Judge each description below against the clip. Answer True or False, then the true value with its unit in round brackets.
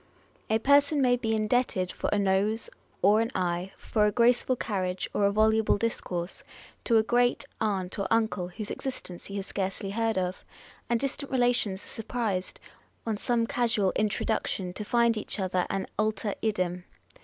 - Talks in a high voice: True (215 Hz)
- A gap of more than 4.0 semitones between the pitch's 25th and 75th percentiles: False (3.4 semitones)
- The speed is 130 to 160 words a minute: False (170 wpm)